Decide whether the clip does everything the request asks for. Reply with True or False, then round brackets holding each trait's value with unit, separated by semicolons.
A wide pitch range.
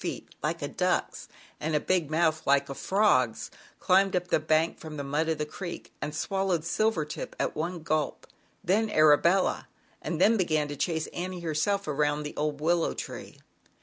False (3.3 semitones)